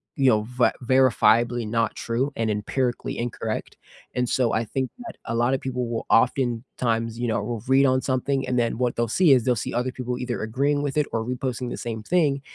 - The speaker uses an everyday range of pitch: No, narrow, 2.2 semitones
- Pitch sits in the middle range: No, low, 125 Hz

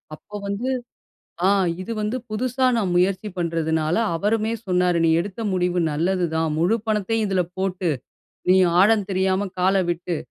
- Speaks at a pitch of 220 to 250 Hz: No, high, 190 Hz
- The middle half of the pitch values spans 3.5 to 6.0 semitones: No, average, 3.1 semitones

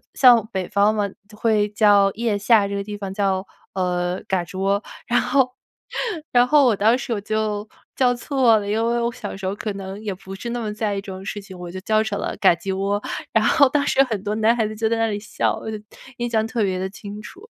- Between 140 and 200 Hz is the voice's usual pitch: No, high, 210 Hz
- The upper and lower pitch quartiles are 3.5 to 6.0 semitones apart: No, average, 2.7 semitones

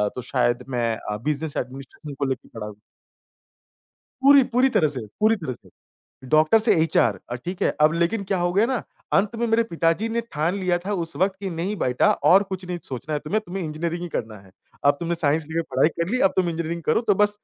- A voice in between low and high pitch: Yes, medium, 170 Hz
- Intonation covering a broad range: Yes, wide, 5.7 semitones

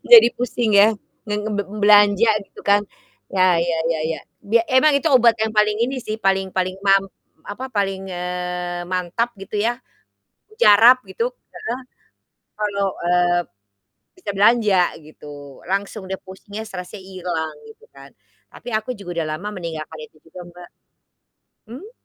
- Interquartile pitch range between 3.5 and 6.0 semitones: Yes, average, 3.8 semitones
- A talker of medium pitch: No, high, 200 Hz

